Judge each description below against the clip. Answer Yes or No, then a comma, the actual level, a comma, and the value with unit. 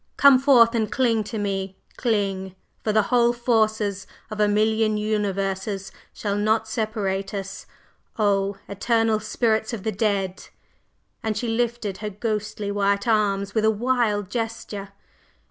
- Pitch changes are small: Yes, narrow, 2.1 semitones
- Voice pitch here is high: Yes, high, 215 Hz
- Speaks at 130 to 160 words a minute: Yes, average, 140 wpm